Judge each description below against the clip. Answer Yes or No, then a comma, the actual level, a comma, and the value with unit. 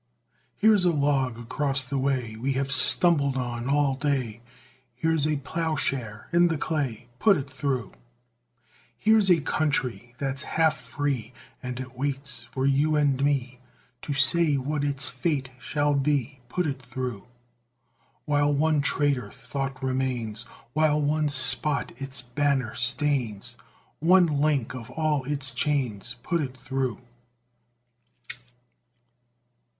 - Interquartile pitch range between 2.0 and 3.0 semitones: Yes, narrow, 2.6 semitones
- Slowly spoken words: Yes, slow, 130 wpm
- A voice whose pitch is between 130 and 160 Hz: Yes, medium, 140 Hz